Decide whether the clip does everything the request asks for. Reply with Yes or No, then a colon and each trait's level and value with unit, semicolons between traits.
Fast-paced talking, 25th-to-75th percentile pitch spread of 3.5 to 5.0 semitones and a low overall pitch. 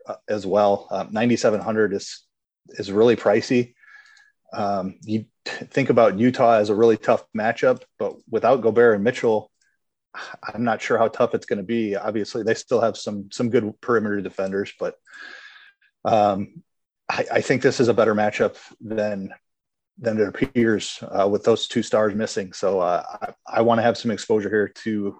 No: average, 175 wpm; average, 4.2 semitones; low, 110 Hz